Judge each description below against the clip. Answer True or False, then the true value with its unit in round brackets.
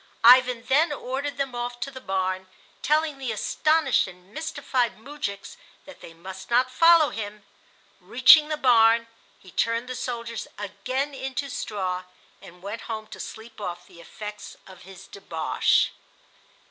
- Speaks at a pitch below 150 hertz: False (235 Hz)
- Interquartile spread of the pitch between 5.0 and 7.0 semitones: True (5.3 semitones)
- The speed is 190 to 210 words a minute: False (145 wpm)